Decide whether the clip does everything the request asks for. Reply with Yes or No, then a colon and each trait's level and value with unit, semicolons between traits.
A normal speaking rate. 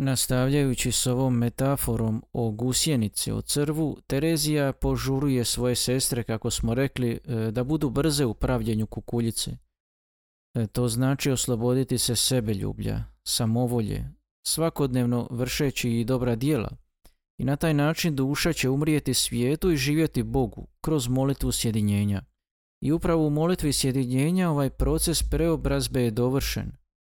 Yes: average, 125 wpm